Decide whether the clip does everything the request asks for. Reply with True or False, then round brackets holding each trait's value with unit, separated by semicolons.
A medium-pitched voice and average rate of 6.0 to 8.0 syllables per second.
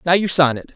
True (160 Hz; 6.4 syllables/s)